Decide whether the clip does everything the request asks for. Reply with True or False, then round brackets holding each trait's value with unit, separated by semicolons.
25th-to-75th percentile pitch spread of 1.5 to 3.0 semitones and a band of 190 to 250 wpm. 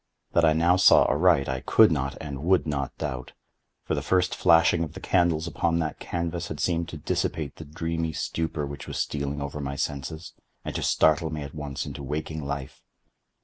True (2.7 semitones; 195 wpm)